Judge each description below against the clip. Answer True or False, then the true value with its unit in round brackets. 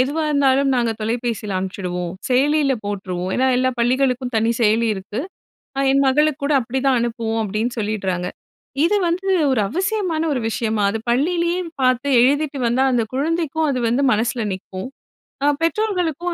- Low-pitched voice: False (255 Hz)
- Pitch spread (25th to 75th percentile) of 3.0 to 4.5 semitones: False (5.2 semitones)